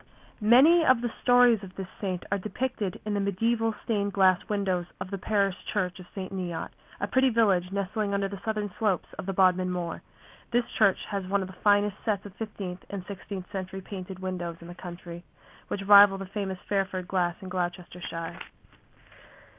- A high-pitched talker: Yes, high, 195 Hz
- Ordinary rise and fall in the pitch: No, narrow, 2.1 semitones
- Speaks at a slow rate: No, average, 185 wpm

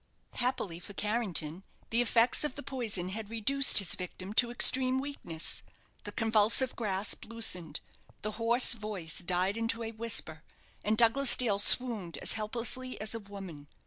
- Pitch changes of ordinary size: Yes, average, 3.8 semitones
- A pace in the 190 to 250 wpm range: No, average, 150 wpm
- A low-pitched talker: No, high, 220 Hz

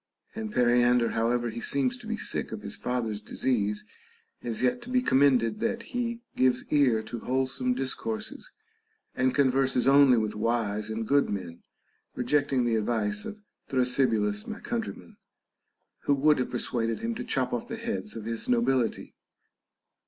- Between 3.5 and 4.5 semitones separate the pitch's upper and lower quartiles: Yes, average, 3.8 semitones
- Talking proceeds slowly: No, average, 155 wpm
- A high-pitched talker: No, low, 125 Hz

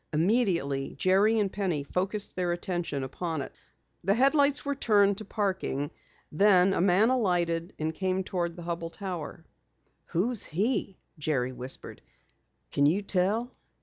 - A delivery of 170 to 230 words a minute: No, average, 145 wpm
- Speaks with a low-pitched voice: No, medium, 185 Hz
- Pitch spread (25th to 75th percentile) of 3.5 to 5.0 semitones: Yes, average, 3.8 semitones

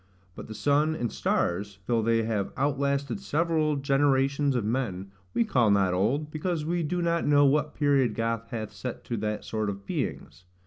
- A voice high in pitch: No, low, 130 Hz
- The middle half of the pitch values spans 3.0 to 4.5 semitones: No, average, 5.3 semitones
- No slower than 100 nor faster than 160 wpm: No, average, 180 wpm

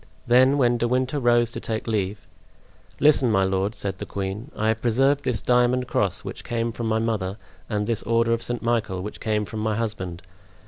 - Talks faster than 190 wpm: Yes, average, 200 wpm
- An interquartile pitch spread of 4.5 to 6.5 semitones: No, narrow, 2.6 semitones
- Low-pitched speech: Yes, low, 115 Hz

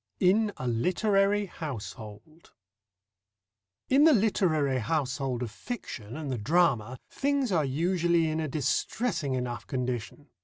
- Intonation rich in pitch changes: Yes, wide, 7.1 semitones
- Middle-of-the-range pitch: Yes, medium, 155 Hz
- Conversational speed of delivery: No, slow, 120 wpm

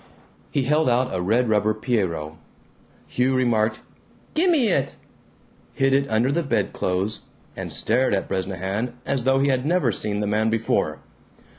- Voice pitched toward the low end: Yes, low, 120 Hz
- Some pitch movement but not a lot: Yes, average, 4.2 semitones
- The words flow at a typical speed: Yes, average, 150 wpm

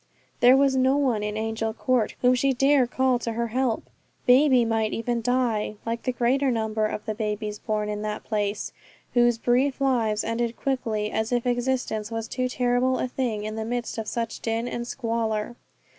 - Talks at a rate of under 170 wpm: No, average, 190 wpm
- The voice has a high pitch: Yes, high, 235 Hz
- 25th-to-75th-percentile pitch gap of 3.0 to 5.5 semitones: No, narrow, 2.5 semitones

